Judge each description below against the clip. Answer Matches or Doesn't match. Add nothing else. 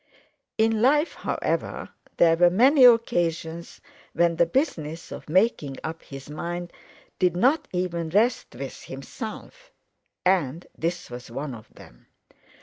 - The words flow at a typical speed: Doesn't match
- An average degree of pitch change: Doesn't match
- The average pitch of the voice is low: Doesn't match